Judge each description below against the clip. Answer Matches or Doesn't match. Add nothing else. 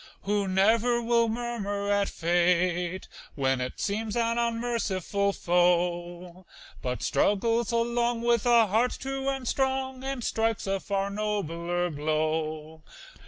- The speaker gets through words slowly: Matches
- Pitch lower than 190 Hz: Doesn't match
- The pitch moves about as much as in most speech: Matches